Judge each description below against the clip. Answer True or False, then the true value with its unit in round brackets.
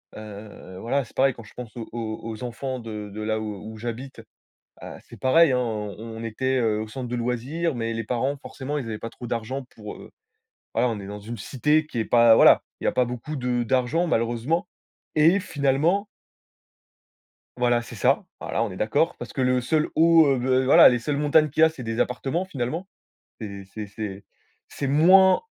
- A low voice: True (125 Hz)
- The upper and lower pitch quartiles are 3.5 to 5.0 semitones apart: True (4.1 semitones)